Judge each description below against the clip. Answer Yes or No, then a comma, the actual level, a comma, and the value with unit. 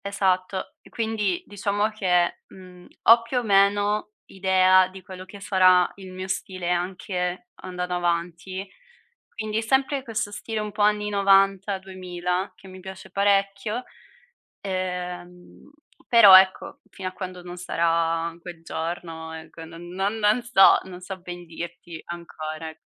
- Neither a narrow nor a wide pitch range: No, narrow, 2.3 semitones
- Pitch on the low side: No, medium, 185 Hz